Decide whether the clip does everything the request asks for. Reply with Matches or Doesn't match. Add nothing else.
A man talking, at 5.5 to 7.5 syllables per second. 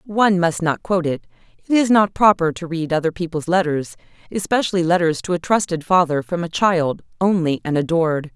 Doesn't match